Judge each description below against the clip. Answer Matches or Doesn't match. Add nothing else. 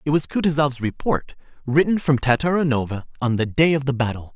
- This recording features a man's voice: Matches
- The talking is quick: Doesn't match